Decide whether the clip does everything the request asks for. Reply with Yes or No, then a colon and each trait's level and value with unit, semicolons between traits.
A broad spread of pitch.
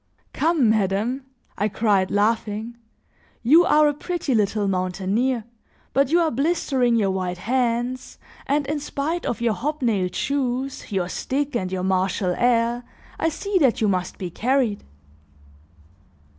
Yes: wide, 5.7 semitones